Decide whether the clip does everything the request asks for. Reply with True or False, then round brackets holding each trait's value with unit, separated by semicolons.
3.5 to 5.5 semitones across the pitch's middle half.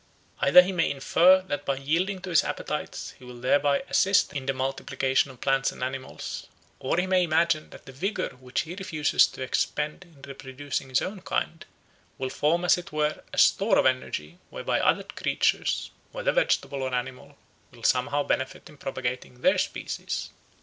True (4.6 semitones)